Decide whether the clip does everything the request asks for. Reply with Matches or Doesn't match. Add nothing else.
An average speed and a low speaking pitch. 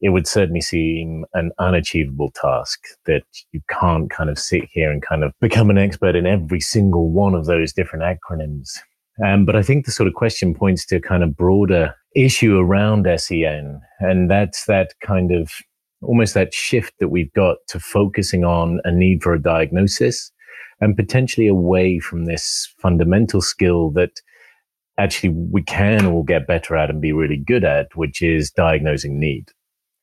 Matches